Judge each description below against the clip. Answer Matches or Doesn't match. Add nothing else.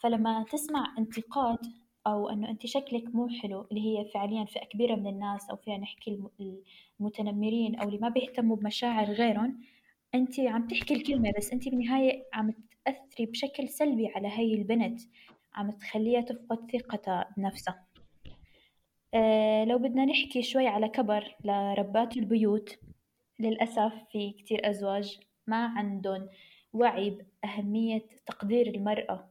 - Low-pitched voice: Doesn't match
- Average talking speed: Doesn't match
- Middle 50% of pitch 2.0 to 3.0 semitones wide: Matches